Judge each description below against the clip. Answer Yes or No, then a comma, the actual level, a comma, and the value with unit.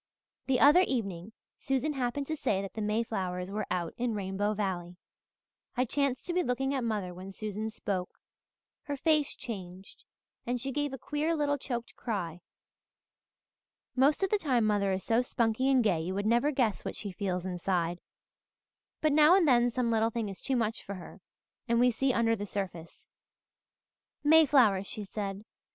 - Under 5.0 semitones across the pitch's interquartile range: No, wide, 5.5 semitones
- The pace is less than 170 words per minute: No, average, 175 wpm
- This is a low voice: No, high, 225 Hz